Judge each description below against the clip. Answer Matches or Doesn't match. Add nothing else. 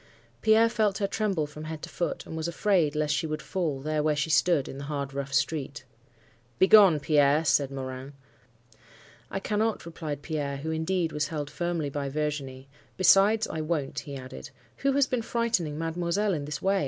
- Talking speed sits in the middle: Matches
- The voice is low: Doesn't match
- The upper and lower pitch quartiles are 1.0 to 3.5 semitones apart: Doesn't match